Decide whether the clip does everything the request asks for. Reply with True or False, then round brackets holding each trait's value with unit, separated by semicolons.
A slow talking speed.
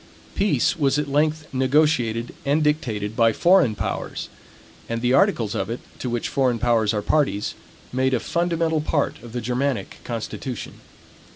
False (155 wpm)